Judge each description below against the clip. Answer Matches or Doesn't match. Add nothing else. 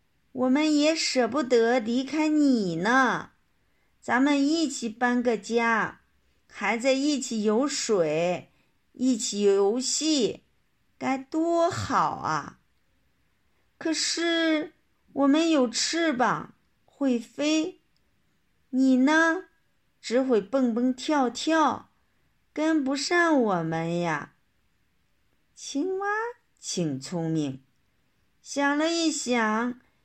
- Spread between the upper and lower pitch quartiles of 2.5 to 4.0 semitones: Doesn't match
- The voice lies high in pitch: Matches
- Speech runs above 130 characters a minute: Doesn't match